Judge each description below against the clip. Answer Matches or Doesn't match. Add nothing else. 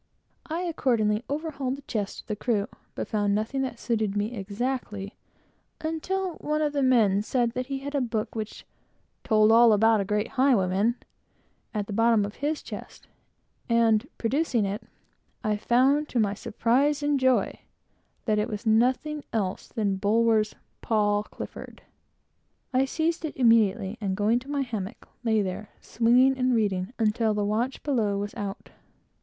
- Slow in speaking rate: Doesn't match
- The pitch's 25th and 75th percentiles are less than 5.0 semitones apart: Matches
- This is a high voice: Matches